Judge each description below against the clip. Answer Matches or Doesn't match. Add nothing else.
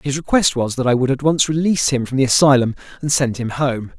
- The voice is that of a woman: Doesn't match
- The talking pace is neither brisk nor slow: Doesn't match